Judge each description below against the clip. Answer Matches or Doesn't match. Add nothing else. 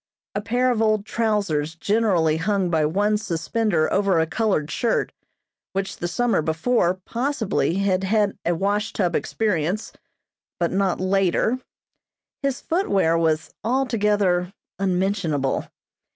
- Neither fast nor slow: Doesn't match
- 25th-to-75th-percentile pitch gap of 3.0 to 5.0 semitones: Matches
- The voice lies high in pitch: Matches